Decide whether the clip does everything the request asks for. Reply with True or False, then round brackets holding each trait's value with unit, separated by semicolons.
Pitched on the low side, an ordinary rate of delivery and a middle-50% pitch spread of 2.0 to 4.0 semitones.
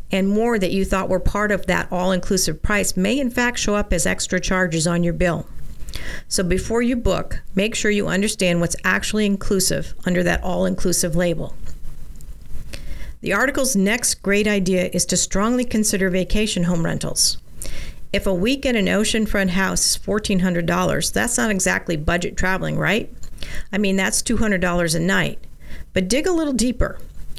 False (190 Hz; 170 wpm; 2.9 semitones)